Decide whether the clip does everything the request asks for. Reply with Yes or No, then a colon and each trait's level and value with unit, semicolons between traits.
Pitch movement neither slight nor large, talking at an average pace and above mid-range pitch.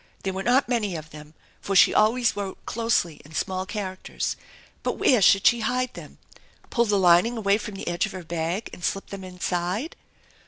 Yes: average, 4.1 semitones; average, 195 wpm; high, 195 Hz